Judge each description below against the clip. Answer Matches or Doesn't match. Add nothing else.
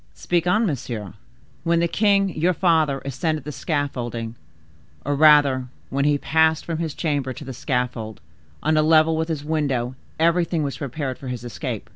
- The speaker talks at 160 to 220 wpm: Matches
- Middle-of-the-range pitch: Matches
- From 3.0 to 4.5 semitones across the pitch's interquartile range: Matches